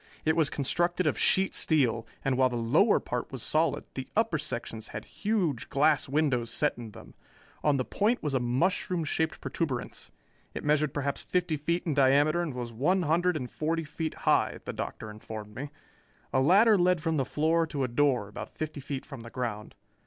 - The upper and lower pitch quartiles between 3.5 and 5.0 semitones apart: Yes, average, 4.6 semitones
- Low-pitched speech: No, medium, 150 Hz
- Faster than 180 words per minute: Yes, average, 195 wpm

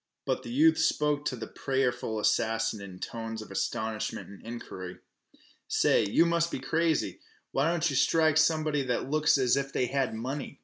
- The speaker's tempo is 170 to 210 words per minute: Yes, average, 175 wpm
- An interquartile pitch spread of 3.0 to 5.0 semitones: No, wide, 5.5 semitones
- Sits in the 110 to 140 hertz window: Yes, low, 135 Hz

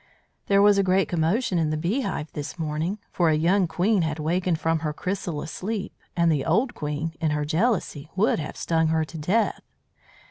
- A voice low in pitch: No, medium, 165 Hz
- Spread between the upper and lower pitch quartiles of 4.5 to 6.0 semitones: No, average, 3.7 semitones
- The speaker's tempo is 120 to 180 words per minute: No, average, 200 wpm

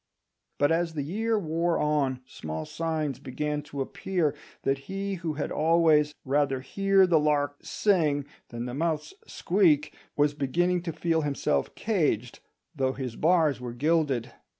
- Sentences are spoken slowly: No, average, 150 wpm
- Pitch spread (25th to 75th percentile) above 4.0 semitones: No, average, 3.6 semitones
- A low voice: No, medium, 150 Hz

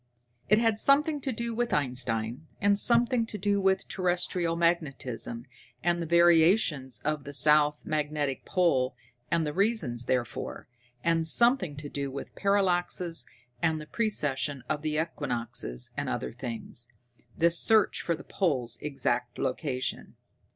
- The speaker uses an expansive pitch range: Yes, wide, 6.2 semitones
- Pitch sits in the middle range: Yes, medium, 160 Hz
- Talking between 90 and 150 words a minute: Yes, average, 140 wpm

